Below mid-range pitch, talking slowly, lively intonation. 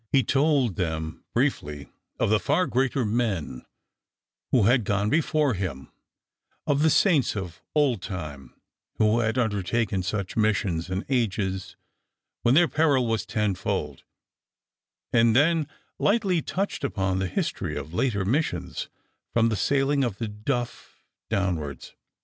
Yes: low, 110 Hz; slow, 130 wpm; wide, 6.4 semitones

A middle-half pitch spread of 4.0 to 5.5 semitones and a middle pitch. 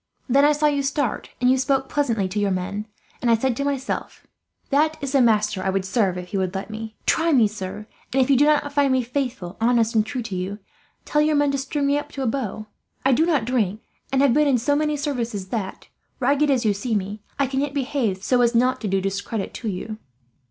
No: average, 5.0 semitones; high, 245 Hz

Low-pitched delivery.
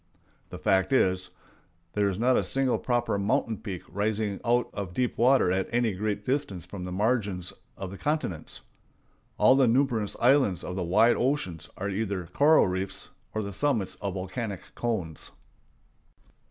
Yes: low, 105 Hz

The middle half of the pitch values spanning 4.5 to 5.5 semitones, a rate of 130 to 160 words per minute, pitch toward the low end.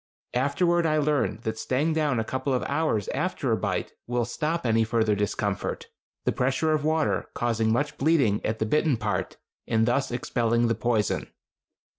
No: average, 5.2 semitones; average, 170 wpm; low, 125 Hz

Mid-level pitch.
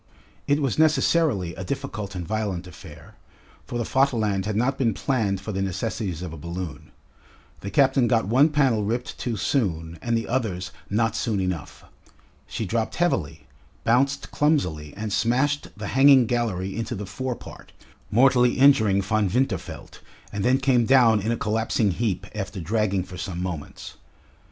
No: low, 110 Hz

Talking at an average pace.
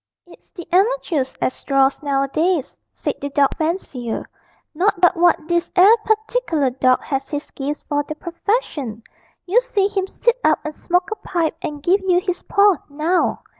Yes: average, 170 wpm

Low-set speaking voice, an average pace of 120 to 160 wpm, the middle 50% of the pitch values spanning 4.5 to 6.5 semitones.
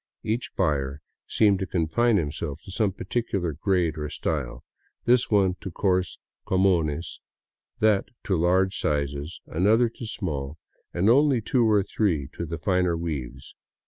Yes: very low, 90 Hz; average, 150 wpm; average, 4.8 semitones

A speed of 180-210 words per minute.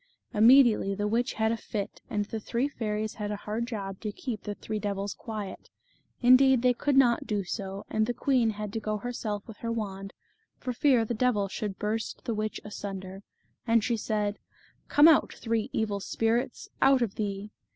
Yes: average, 190 wpm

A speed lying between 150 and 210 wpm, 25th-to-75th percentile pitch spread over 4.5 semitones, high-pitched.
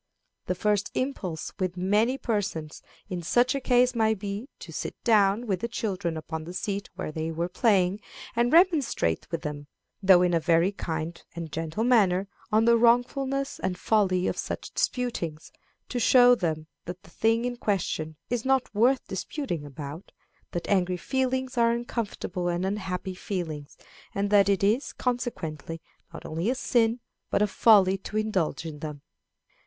Yes: average, 165 wpm; wide, 5.6 semitones; high, 200 Hz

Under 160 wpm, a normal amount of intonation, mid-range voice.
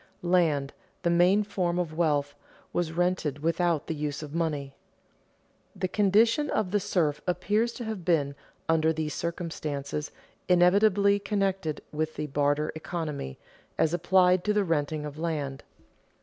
Yes: average, 145 wpm; average, 3.7 semitones; medium, 170 Hz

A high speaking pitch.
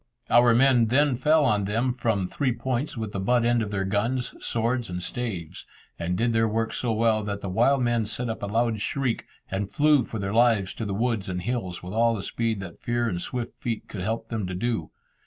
No: low, 115 Hz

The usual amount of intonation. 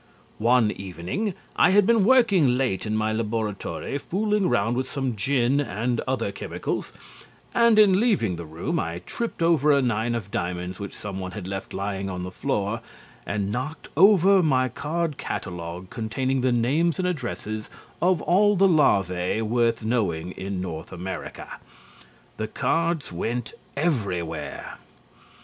No: wide, 8.8 semitones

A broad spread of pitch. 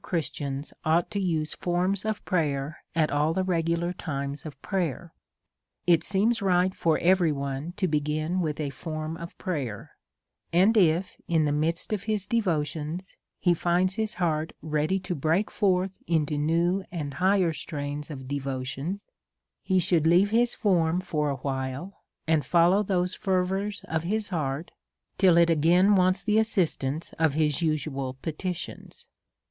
No: average, 3.7 semitones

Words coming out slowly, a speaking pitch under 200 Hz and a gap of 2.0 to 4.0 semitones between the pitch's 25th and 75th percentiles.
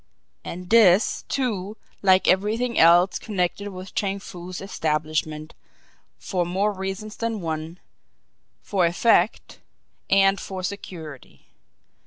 Yes: slow, 105 wpm; high, 190 Hz; average, 2.9 semitones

